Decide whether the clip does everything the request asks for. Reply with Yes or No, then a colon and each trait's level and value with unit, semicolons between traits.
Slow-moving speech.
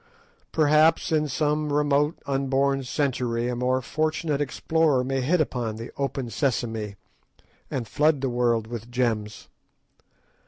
Yes: slow, 125 wpm